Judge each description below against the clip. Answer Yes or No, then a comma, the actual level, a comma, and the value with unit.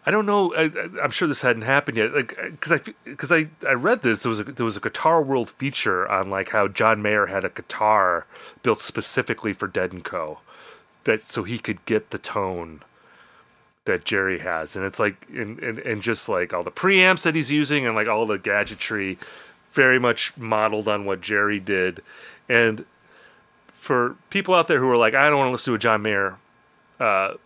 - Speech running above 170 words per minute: Yes, fast, 205 wpm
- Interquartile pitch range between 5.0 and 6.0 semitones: Yes, average, 5.3 semitones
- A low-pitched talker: Yes, low, 115 Hz